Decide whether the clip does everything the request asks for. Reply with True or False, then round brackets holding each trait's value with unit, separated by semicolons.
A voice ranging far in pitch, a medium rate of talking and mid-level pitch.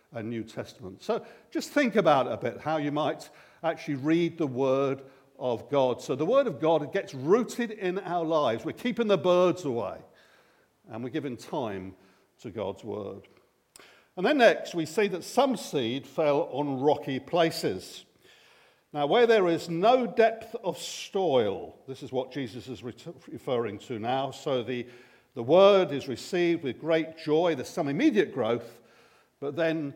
True (6.4 semitones; 165 wpm; 160 Hz)